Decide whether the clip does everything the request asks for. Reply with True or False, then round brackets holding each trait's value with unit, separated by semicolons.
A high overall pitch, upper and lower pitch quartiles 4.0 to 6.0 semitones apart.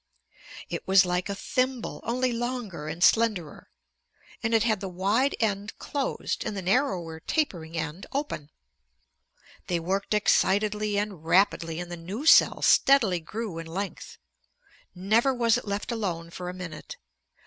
True (200 Hz; 4.8 semitones)